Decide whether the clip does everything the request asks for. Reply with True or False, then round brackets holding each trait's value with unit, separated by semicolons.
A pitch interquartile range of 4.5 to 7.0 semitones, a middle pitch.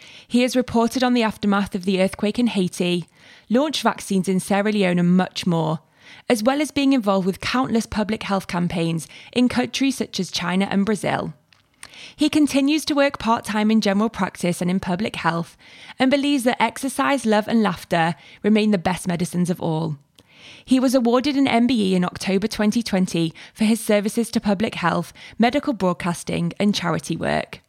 False (5.1 semitones; 205 Hz)